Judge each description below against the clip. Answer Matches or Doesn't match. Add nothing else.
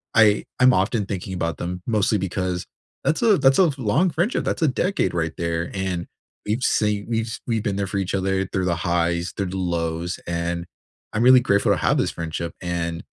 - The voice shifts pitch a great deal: Doesn't match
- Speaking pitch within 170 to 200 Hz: Doesn't match